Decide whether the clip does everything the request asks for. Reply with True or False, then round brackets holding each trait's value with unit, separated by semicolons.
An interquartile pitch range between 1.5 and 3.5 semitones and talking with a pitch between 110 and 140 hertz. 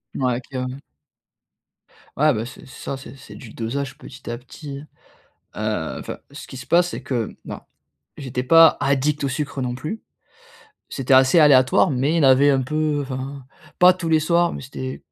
True (2.8 semitones; 135 Hz)